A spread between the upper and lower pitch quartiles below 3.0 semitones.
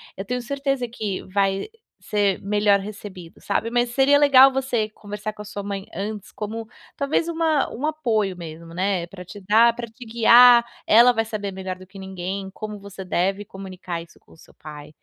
No: average, 3.7 semitones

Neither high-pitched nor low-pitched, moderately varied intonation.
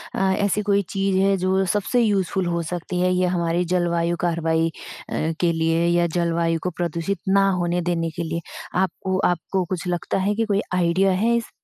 No: medium, 180 Hz; narrow, 2.3 semitones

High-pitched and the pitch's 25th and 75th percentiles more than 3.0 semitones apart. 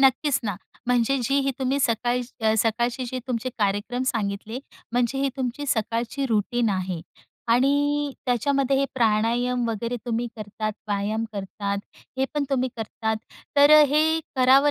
Yes: high, 240 Hz; average, 3.4 semitones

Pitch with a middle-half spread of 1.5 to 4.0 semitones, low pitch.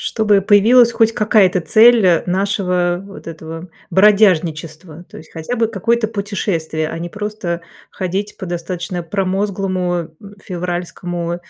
No: average, 3.3 semitones; medium, 185 Hz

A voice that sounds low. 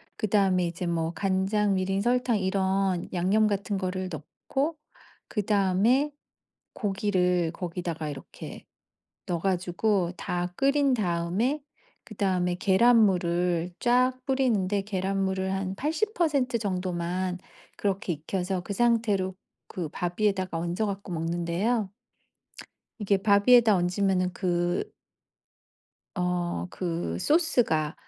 No: high, 190 Hz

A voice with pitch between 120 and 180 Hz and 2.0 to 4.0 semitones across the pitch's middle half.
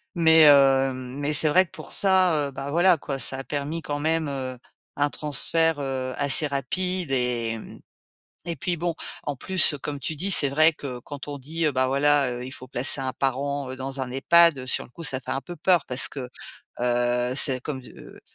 Yes: medium, 140 Hz; average, 3.6 semitones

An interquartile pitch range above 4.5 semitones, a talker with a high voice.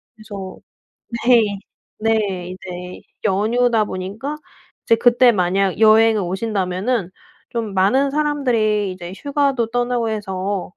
No: average, 4.2 semitones; high, 215 Hz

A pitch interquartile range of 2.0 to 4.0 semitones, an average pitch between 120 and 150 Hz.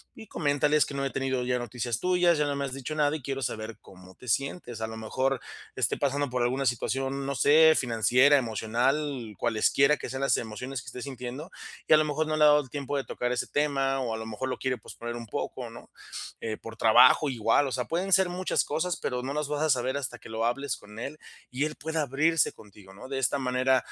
Yes: average, 3.3 semitones; low, 135 Hz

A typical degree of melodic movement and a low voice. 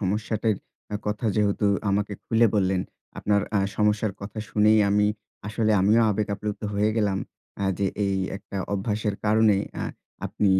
No: narrow, 1.3 semitones; low, 105 Hz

